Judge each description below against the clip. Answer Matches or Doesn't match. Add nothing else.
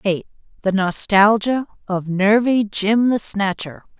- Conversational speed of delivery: Doesn't match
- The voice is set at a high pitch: Matches